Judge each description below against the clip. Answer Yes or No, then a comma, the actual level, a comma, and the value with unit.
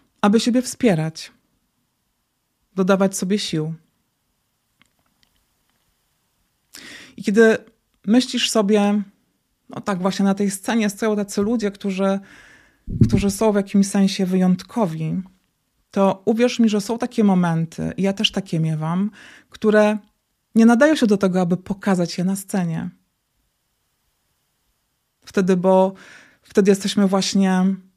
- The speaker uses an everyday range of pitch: No, narrow, 2.2 semitones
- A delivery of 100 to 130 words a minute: Yes, average, 115 wpm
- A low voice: No, high, 200 Hz